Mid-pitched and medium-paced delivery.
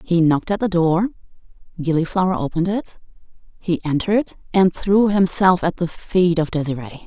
Yes: medium, 180 Hz; average, 155 wpm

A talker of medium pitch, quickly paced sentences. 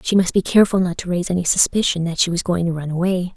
Yes: medium, 180 Hz; fast, 285 wpm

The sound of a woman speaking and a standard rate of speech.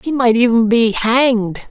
No: male; average, 175 wpm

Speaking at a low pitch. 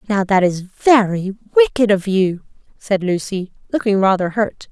No: high, 205 Hz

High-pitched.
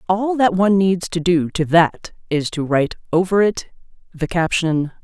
No: medium, 175 Hz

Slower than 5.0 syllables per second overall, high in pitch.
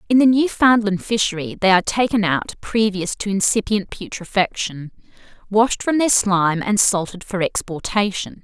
Yes: 4.8 syllables/s; high, 200 Hz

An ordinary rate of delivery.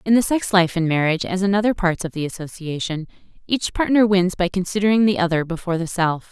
No: fast, 220 wpm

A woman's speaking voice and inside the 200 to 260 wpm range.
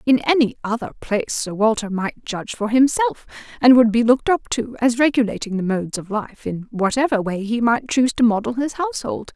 Yes: female; fast, 205 wpm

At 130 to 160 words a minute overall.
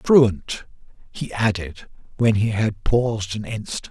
Yes: average, 140 wpm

